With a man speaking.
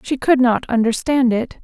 No: female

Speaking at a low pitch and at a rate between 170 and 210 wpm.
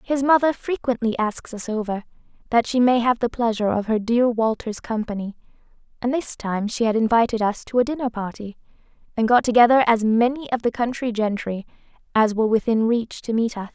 No: high, 230 Hz; average, 190 wpm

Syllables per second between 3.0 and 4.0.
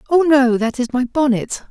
No: 5.0 syllables/s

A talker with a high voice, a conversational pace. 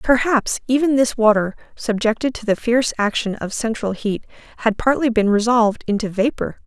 Yes: high, 230 Hz; average, 160 wpm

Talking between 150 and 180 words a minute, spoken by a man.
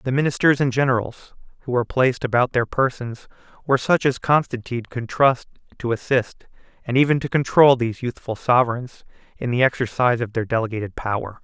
Yes: average, 170 wpm; male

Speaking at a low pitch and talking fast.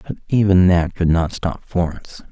No: very low, 90 Hz; average, 180 wpm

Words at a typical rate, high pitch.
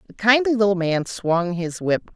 Yes: average, 195 wpm; high, 195 Hz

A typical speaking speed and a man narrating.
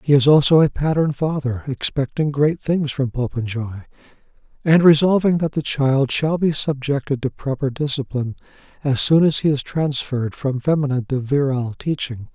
Yes: average, 160 wpm; male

